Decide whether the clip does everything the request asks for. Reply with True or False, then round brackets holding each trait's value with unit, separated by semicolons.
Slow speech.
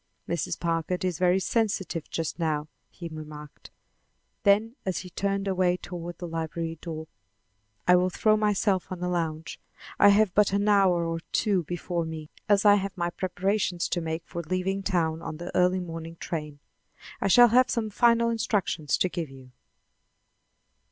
False (165 wpm)